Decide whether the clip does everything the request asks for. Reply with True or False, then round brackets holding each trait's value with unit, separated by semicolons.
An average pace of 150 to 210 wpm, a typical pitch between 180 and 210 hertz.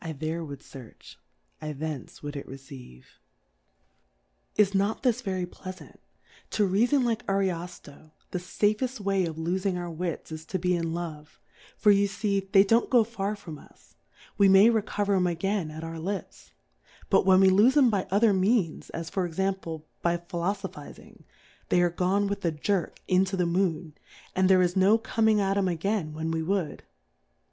True (170 wpm; 185 Hz)